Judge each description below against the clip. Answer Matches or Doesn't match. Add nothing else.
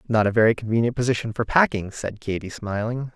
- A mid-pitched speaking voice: Doesn't match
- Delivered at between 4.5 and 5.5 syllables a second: Doesn't match